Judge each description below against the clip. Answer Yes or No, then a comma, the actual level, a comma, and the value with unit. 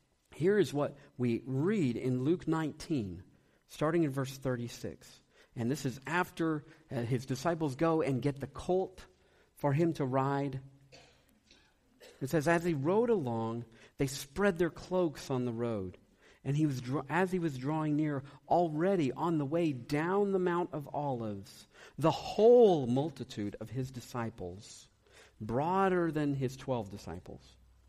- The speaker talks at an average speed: Yes, average, 150 wpm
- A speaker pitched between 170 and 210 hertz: No, medium, 140 Hz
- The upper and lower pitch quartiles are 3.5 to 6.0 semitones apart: Yes, average, 5.2 semitones